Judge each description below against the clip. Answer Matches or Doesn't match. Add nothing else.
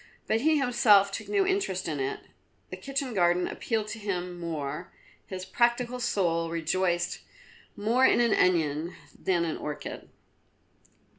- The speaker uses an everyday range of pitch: Doesn't match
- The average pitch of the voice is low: Doesn't match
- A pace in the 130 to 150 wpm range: Matches